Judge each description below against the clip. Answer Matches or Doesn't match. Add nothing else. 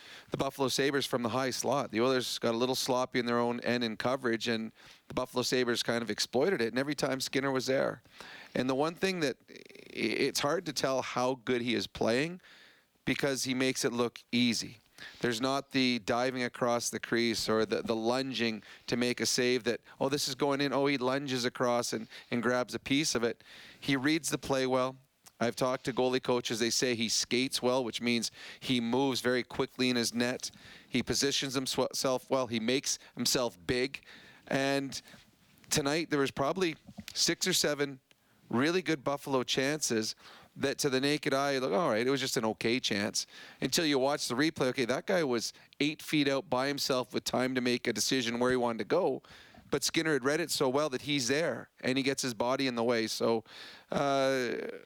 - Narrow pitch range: Matches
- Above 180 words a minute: Matches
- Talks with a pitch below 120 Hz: Doesn't match